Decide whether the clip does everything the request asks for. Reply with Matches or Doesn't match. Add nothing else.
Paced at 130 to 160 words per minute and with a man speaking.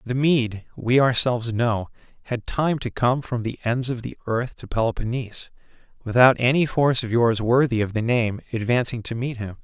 Doesn't match